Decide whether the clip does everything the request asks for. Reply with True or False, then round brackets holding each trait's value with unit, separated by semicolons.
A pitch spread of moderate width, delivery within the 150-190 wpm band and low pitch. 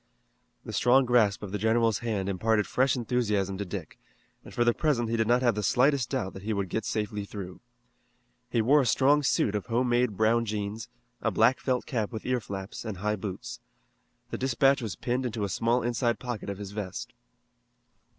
False (3.2 semitones; 200 wpm; 115 Hz)